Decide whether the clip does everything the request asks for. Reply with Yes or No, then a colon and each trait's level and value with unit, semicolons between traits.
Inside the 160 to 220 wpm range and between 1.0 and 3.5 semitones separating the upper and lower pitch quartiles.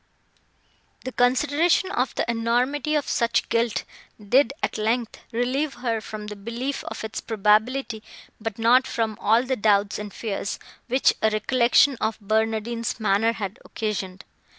No: average, 145 wpm; average, 2.9 semitones